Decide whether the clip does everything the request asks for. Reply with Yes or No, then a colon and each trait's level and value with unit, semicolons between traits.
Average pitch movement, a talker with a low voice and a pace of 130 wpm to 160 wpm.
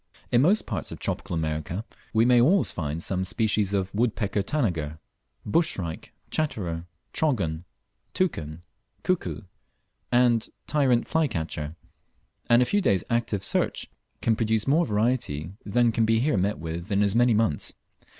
No: wide, 5.7 semitones; low, 110 Hz; average, 145 wpm